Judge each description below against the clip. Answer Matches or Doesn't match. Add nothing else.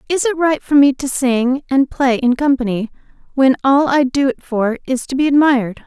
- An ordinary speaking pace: Doesn't match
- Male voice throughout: Doesn't match